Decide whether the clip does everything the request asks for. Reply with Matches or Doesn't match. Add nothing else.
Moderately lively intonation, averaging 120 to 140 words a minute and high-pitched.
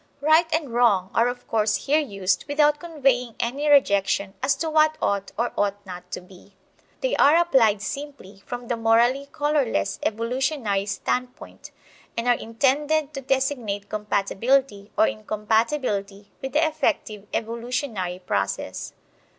Doesn't match